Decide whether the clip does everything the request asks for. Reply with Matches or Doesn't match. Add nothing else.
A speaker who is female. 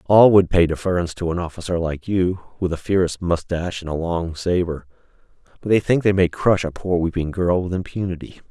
Doesn't match